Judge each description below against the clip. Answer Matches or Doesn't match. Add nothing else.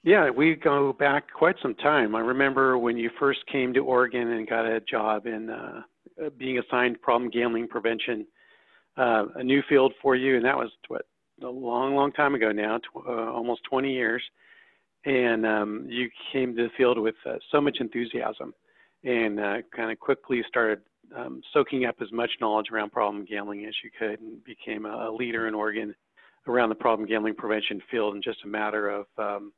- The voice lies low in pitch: Matches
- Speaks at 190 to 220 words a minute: Matches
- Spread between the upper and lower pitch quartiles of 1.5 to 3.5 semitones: Matches